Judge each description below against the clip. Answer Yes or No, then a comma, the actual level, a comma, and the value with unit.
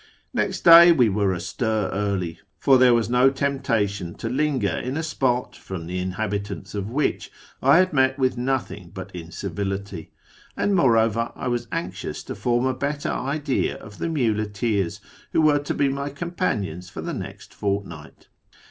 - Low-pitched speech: Yes, low, 115 Hz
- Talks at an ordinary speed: Yes, average, 165 wpm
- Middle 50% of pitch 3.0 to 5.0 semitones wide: No, wide, 5.6 semitones